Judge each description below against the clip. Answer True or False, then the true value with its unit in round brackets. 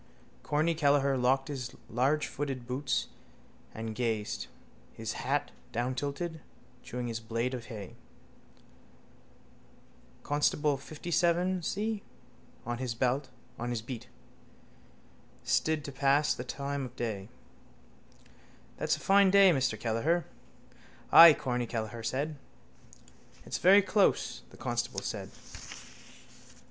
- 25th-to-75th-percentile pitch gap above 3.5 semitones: True (4.2 semitones)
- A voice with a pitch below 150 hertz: True (135 Hz)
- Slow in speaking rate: True (100 wpm)